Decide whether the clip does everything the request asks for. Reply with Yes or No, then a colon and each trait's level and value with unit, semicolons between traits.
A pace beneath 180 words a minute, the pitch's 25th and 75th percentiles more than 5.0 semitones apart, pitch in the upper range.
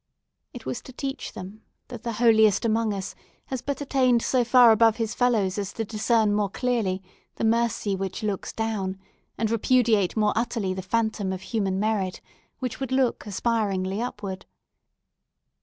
No: average, 160 wpm; average, 3.1 semitones; high, 220 Hz